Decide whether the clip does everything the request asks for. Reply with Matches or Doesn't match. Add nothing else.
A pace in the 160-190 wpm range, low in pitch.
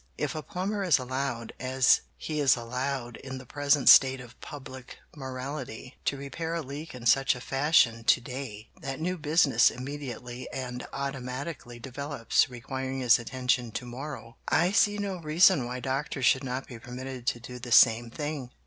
Matches